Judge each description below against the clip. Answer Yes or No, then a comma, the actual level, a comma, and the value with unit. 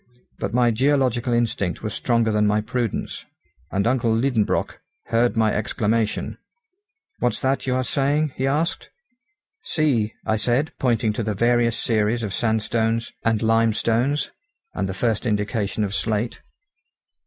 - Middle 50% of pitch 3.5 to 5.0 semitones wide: No, narrow, 2.4 semitones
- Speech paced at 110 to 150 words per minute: Yes, average, 140 wpm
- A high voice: No, low, 115 Hz